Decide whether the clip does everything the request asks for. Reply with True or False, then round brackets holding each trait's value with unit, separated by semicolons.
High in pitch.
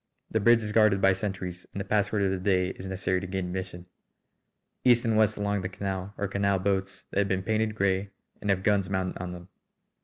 False (95 Hz)